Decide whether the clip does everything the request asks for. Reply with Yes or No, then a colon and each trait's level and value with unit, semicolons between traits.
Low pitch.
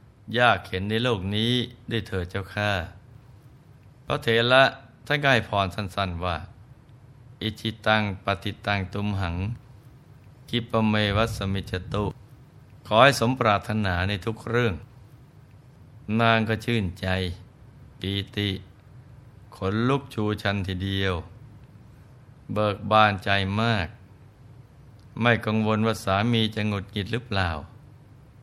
Yes: low, 110 Hz